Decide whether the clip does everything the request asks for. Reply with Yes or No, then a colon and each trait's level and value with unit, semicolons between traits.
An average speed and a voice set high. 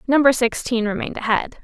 Yes: average, 145 wpm; high, 240 Hz